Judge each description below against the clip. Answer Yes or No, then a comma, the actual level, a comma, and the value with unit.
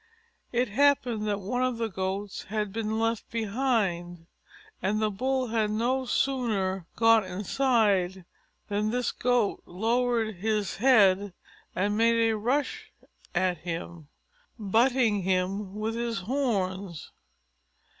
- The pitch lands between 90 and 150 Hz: No, high, 215 Hz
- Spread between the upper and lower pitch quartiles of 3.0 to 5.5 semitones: Yes, average, 3.8 semitones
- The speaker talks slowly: Yes, slow, 120 wpm